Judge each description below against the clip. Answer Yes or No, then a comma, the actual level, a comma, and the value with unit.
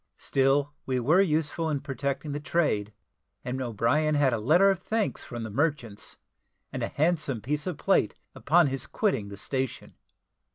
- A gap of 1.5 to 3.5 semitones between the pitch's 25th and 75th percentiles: No, average, 4.0 semitones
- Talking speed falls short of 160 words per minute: No, average, 165 wpm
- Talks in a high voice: No, medium, 140 Hz